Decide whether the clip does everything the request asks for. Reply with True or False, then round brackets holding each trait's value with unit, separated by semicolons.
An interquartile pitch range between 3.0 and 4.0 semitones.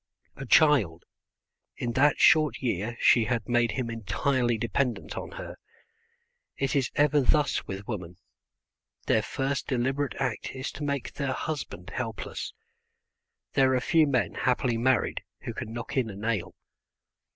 True (3.4 semitones)